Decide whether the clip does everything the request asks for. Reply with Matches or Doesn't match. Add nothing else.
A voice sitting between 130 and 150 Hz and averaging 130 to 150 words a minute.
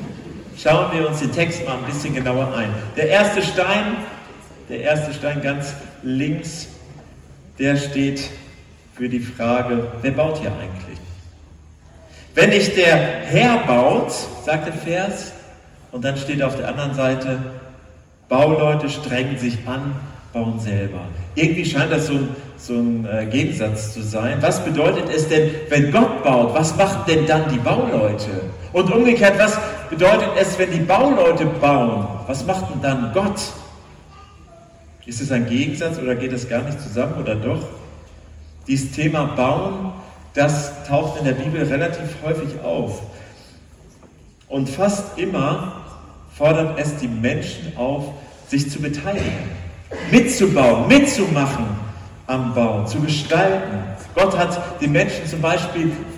Matches